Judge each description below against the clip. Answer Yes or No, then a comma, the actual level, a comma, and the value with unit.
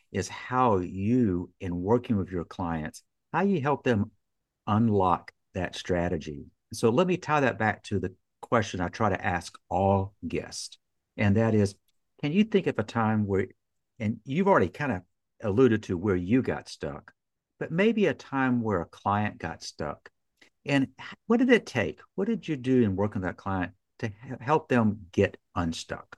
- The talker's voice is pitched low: Yes, low, 105 Hz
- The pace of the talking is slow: No, average, 180 wpm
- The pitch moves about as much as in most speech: No, wide, 5.8 semitones